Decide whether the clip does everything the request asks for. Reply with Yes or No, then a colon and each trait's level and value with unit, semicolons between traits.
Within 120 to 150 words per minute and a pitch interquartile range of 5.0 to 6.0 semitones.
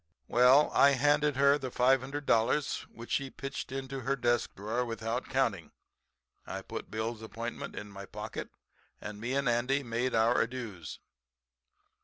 No: average, 145 wpm; average, 3.3 semitones